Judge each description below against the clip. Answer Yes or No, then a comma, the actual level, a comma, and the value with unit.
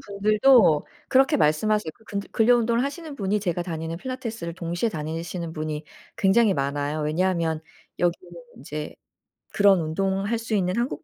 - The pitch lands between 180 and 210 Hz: Yes, high, 190 Hz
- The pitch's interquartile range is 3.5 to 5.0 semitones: No, wide, 5.5 semitones